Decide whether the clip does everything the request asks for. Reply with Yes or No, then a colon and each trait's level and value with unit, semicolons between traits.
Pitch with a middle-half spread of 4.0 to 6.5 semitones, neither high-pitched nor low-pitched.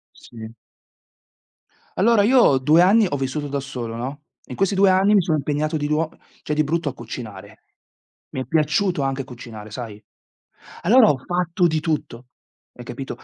Yes: wide, 5.6 semitones; medium, 150 Hz